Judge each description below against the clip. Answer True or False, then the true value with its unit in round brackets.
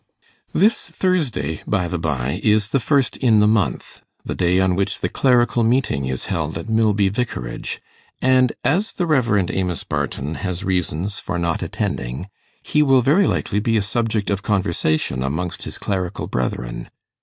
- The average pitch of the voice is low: True (100 Hz)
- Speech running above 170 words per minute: False (165 wpm)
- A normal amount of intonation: False (5.9 semitones)